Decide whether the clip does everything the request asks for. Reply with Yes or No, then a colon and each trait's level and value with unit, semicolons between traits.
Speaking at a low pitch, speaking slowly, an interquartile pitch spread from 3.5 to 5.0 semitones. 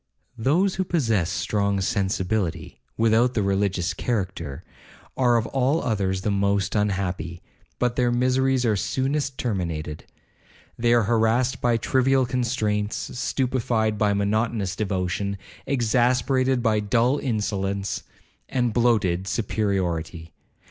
Yes: low, 110 Hz; slow, 115 wpm; average, 4.1 semitones